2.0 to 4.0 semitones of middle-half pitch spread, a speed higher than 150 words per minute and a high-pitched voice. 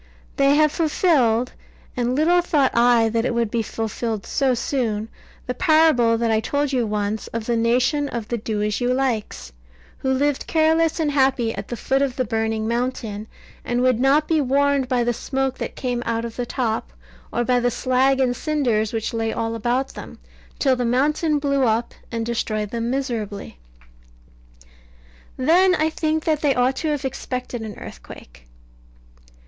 Yes: average, 3.6 semitones; average, 175 wpm; very high, 250 Hz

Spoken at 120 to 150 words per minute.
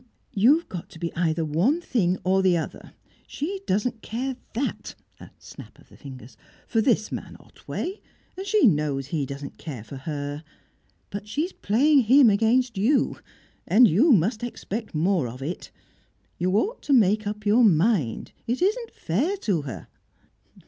No: average, 160 wpm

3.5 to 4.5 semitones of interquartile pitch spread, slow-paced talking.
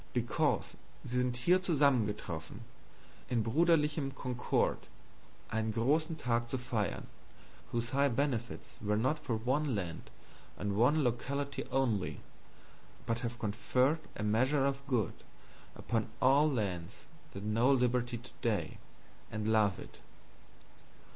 Yes: average, 3.9 semitones; slow, 115 wpm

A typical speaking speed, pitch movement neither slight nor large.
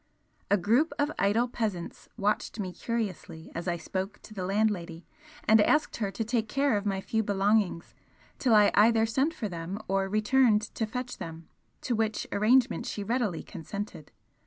Yes: average, 170 wpm; average, 3.1 semitones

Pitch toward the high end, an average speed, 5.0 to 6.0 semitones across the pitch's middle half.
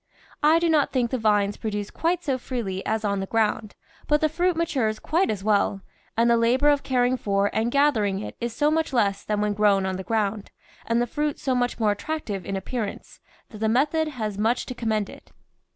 No: high, 230 Hz; fast, 220 wpm; average, 5.3 semitones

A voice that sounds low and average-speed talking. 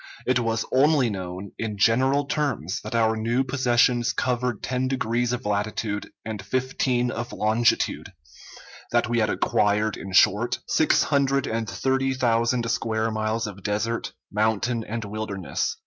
Yes: low, 115 Hz; average, 145 wpm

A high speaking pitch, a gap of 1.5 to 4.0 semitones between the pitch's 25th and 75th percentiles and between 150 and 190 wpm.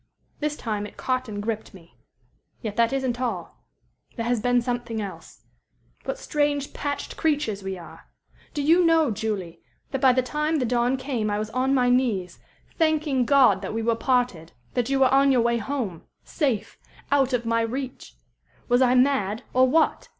Yes: high, 245 Hz; average, 3.7 semitones; average, 180 wpm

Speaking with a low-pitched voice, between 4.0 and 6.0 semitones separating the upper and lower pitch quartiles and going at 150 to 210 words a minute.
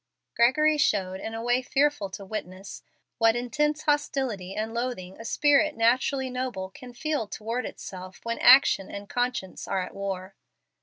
No: high, 230 Hz; average, 5.1 semitones; average, 155 wpm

